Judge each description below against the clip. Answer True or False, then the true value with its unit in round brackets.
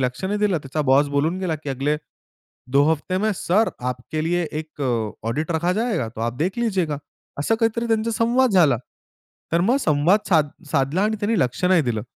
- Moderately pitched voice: True (165 Hz)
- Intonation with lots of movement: True (6.5 semitones)